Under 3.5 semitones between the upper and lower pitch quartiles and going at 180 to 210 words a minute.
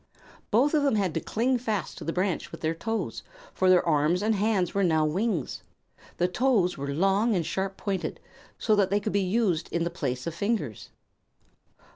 No: average, 4.5 semitones; average, 195 wpm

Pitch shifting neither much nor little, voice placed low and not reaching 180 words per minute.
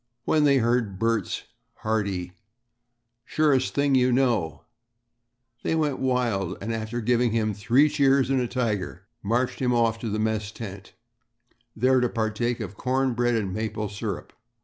Yes: average, 3.1 semitones; low, 115 Hz; average, 150 wpm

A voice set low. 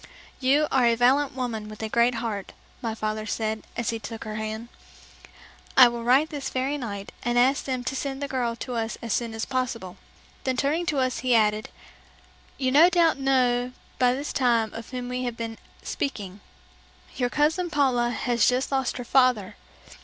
No: high, 245 Hz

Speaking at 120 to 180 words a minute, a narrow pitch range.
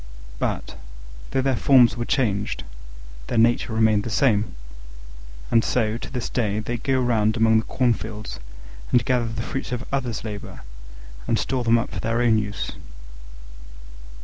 Yes: average, 155 wpm; narrow, 2.2 semitones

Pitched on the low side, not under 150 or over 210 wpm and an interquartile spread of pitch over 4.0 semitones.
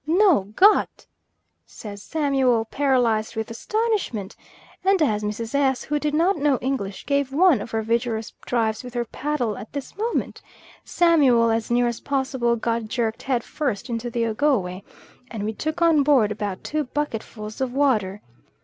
No: high, 245 Hz; average, 160 wpm; average, 4.7 semitones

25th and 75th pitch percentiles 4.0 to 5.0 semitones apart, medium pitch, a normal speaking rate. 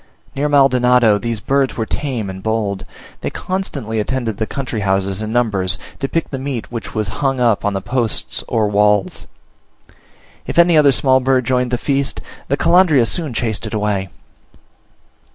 No: average, 4.4 semitones; low, 120 Hz; average, 170 wpm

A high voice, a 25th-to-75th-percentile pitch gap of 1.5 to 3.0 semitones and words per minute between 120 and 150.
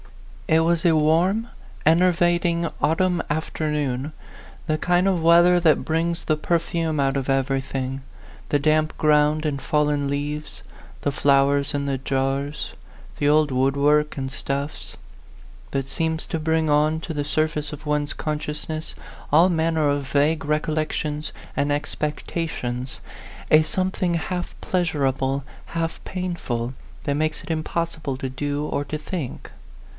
No: medium, 150 Hz; narrow, 2.4 semitones; average, 140 wpm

